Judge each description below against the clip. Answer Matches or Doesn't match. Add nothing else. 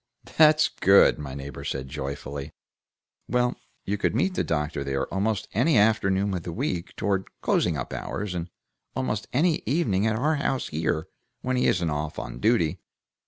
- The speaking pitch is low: Matches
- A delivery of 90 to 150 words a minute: Doesn't match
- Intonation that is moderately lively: Doesn't match